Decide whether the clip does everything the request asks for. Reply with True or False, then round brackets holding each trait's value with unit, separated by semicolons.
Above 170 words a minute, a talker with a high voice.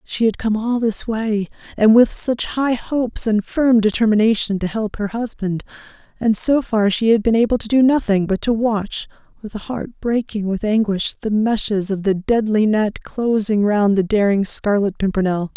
True (190 wpm; 215 Hz)